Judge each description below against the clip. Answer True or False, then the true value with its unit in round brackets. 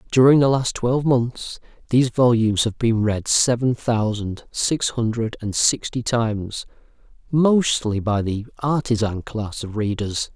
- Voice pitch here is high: False (115 Hz)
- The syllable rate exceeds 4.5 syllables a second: False (4.3 syllables/s)